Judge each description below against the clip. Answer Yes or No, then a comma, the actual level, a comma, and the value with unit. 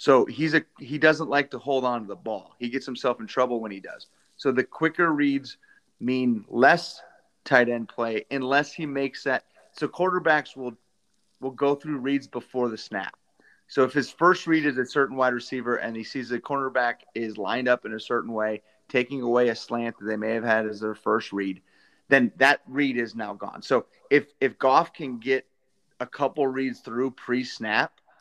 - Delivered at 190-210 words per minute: Yes, average, 200 wpm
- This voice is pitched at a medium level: No, low, 130 Hz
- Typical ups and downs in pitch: Yes, average, 3.2 semitones